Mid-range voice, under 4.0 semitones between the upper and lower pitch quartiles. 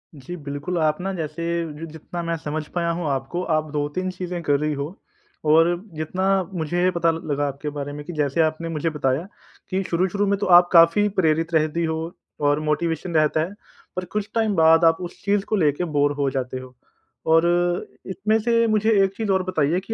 Yes: medium, 165 Hz; average, 3.3 semitones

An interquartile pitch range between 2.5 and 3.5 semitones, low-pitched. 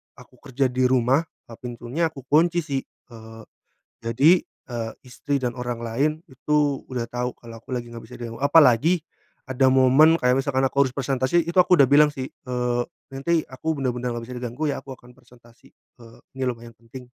Yes: average, 2.8 semitones; low, 130 Hz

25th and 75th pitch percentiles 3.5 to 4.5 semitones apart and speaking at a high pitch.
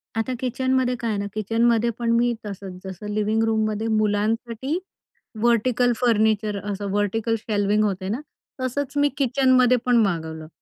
No: average, 3.0 semitones; high, 225 Hz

